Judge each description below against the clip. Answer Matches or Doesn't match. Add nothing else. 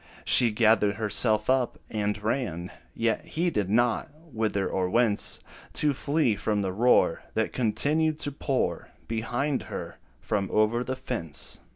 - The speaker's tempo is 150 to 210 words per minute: Doesn't match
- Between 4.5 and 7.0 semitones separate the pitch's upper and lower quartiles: Doesn't match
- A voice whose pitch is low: Matches